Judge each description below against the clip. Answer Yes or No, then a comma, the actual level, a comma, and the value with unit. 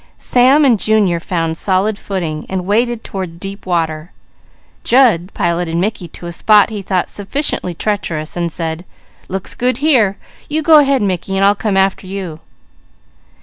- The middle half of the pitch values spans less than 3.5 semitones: No, average, 4.0 semitones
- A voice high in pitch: Yes, high, 195 Hz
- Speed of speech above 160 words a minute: No, average, 155 wpm